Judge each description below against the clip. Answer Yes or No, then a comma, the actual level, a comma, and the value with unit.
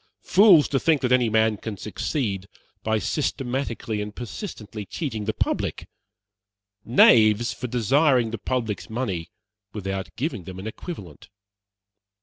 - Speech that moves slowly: Yes, slow, 130 wpm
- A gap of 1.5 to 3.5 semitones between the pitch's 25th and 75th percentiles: No, average, 3.9 semitones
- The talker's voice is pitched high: No, low, 110 Hz